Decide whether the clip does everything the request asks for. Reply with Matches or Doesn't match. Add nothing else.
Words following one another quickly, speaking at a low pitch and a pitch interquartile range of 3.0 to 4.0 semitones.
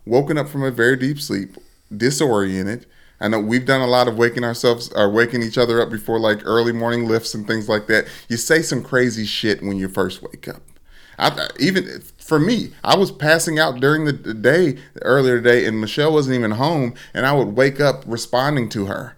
Matches